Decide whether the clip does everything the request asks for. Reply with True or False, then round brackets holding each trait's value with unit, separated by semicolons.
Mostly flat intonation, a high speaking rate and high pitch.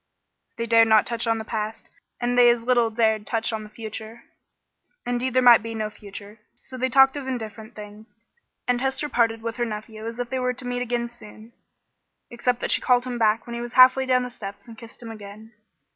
True (2.1 semitones; 220 wpm; 230 Hz)